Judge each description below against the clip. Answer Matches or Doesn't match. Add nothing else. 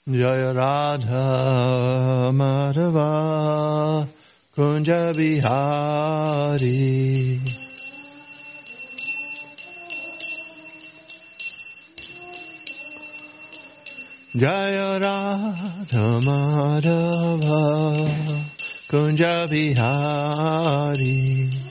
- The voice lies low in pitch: Doesn't match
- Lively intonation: Matches